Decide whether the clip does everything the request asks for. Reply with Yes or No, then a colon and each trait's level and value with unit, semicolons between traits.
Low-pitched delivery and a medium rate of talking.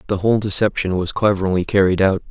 Yes: very low, 95 Hz; average, 180 wpm